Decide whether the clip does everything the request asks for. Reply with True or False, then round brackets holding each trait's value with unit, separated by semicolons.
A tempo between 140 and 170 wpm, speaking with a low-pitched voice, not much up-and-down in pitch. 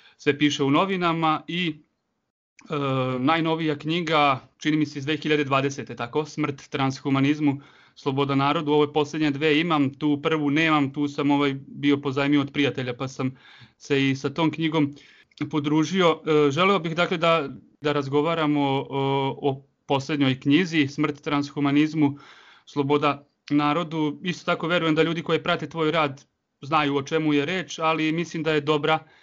False (155 wpm; 150 Hz; 1.9 semitones)